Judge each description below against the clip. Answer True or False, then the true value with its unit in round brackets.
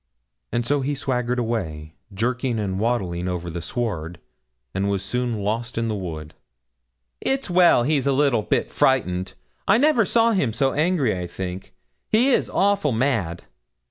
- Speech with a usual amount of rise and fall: False (6.8 semitones)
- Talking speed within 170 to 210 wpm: False (160 wpm)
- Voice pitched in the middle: False (115 Hz)